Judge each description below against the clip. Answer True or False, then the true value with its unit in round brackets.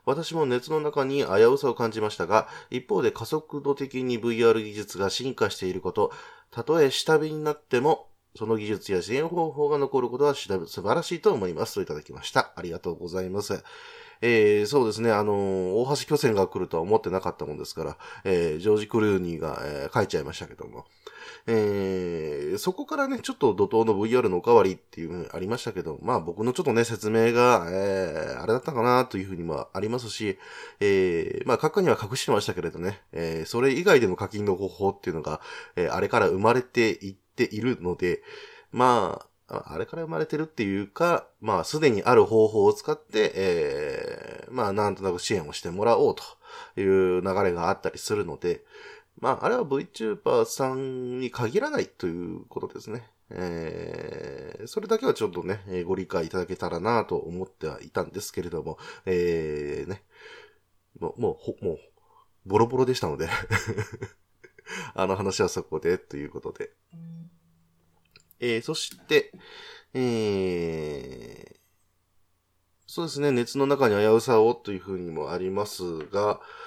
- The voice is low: True (125 Hz)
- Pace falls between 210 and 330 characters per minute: False (355 characters per minute)